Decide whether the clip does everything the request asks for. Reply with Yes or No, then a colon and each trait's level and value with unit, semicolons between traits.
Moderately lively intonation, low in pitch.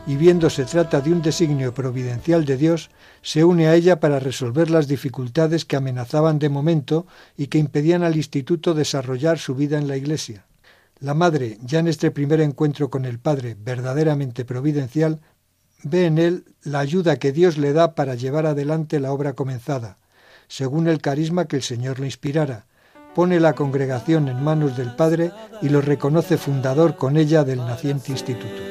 No: average, 3.1 semitones; medium, 150 Hz